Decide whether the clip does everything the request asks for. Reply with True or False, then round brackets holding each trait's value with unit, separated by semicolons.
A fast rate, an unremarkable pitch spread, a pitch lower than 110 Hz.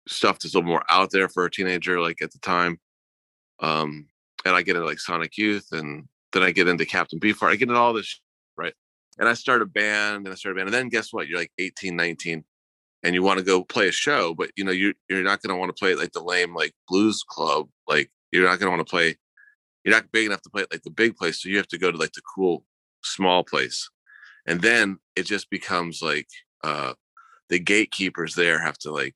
True (250 wpm; 3.7 semitones; 95 Hz)